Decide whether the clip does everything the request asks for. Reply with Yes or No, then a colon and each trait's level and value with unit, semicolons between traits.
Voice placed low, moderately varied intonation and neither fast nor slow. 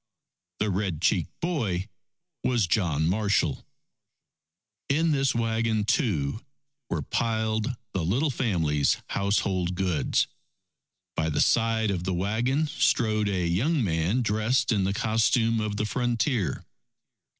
No: low, 105 Hz; average, 4.3 semitones; slow, 120 wpm